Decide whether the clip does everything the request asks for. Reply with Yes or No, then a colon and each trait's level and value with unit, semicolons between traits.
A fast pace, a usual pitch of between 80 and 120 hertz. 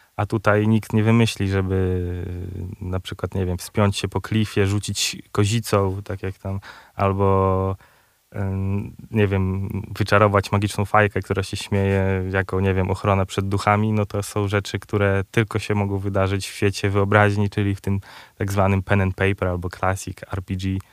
Yes: fast, 165 wpm; low, 100 Hz